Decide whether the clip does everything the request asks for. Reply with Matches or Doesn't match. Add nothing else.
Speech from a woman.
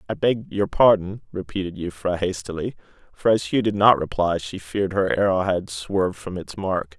Doesn't match